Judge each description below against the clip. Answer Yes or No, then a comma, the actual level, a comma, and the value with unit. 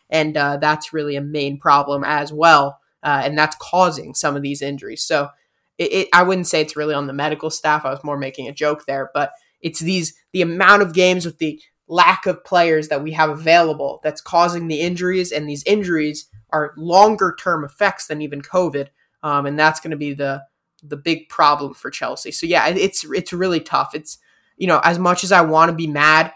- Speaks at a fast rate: Yes, fast, 215 wpm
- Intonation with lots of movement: No, average, 3.0 semitones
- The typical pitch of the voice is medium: Yes, medium, 155 Hz